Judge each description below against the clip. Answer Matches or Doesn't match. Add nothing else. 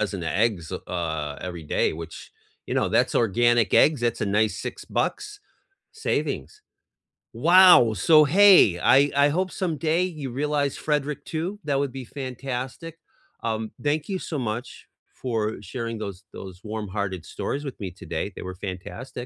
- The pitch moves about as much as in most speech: Doesn't match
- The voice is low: Matches